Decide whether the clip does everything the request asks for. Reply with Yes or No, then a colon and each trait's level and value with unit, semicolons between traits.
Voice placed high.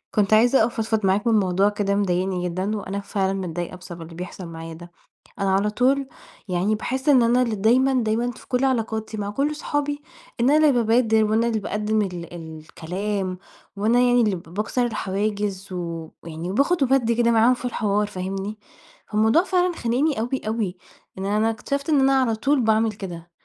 Yes: high, 215 Hz